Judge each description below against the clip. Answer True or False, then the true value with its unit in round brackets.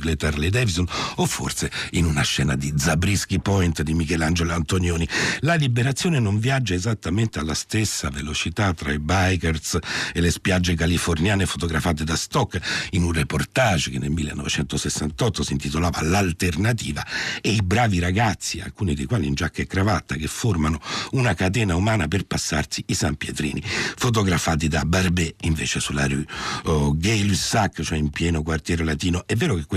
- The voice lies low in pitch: True (85 Hz)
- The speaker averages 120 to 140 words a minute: False (160 wpm)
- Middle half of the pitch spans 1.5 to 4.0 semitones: False (4.4 semitones)